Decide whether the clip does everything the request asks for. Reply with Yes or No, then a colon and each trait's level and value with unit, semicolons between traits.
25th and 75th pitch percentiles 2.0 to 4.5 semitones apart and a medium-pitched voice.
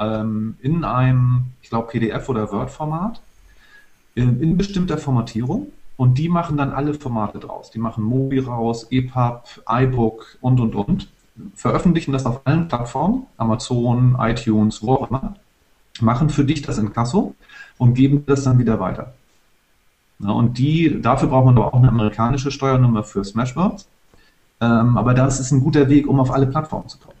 No: average, 3.7 semitones; low, 125 Hz